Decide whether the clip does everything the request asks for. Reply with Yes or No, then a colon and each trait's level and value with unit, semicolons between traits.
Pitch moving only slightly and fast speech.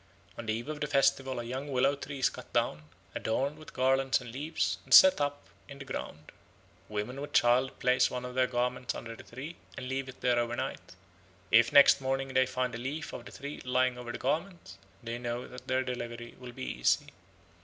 Yes: narrow, 2.2 semitones; fast, 215 wpm